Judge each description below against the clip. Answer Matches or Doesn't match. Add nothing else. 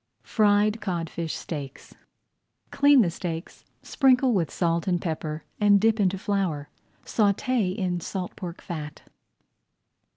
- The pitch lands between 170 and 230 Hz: Matches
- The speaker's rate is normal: Doesn't match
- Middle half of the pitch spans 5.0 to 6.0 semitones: Doesn't match